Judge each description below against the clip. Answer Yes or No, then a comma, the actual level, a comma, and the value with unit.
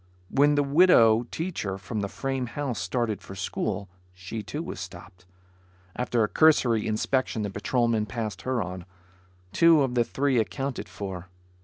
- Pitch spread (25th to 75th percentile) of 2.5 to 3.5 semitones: No, average, 5.2 semitones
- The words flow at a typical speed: Yes, average, 155 wpm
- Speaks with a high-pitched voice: No, low, 115 Hz